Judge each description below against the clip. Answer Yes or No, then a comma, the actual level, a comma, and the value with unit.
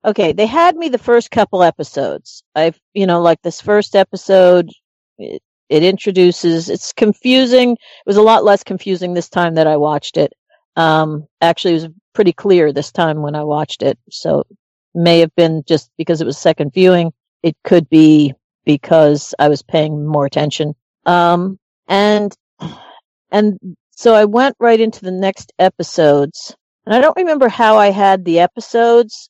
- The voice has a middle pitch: Yes, medium, 175 Hz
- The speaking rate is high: No, average, 170 wpm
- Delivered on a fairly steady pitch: No, average, 4.8 semitones